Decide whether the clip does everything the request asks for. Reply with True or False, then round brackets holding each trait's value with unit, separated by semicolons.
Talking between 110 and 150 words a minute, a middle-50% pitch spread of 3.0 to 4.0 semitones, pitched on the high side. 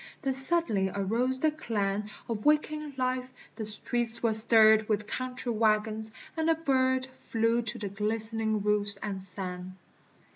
True (145 wpm; 3.6 semitones; 225 Hz)